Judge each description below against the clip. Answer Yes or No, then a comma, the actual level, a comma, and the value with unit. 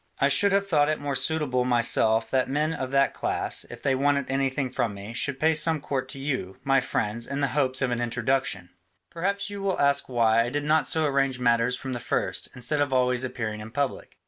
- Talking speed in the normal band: No, fast, 225 wpm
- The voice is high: No, low, 135 Hz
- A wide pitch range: No, average, 3.1 semitones